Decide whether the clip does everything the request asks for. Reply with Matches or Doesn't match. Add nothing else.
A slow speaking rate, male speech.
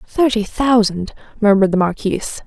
Doesn't match